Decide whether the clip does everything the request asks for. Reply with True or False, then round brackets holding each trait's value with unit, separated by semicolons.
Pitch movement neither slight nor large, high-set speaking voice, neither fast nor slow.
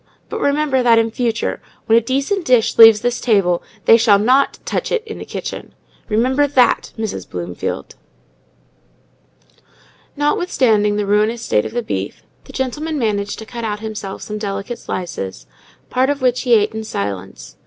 True (3.9 semitones; 225 Hz; 160 wpm)